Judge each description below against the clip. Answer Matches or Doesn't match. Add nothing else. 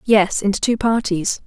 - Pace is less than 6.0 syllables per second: Matches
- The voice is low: Doesn't match